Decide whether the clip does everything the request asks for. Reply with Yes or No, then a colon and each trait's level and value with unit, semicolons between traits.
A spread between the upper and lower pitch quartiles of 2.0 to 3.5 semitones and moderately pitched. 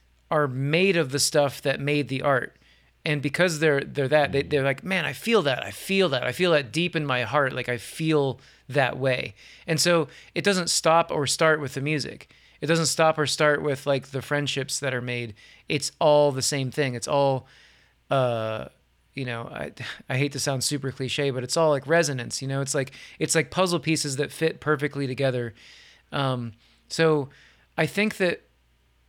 Yes: average, 3.2 semitones; medium, 145 Hz